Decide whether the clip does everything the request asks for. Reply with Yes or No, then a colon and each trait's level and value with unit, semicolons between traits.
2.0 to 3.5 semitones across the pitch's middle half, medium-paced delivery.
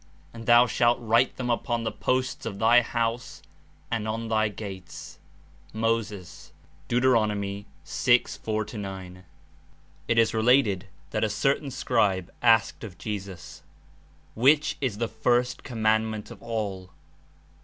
No: narrow, 2.6 semitones; slow, 125 wpm